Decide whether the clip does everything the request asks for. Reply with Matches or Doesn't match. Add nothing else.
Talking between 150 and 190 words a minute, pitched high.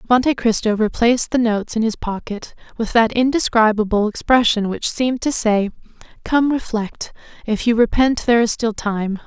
Matches